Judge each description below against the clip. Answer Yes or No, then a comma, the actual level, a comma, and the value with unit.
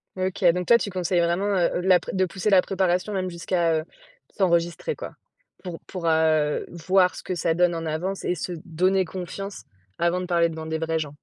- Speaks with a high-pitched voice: No, medium, 175 Hz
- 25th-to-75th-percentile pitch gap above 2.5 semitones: No, narrow, 2.1 semitones